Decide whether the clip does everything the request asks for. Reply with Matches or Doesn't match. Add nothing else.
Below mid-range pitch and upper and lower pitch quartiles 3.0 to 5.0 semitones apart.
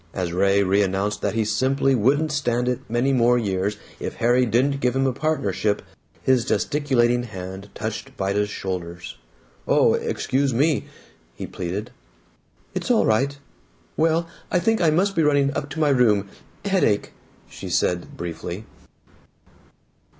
Doesn't match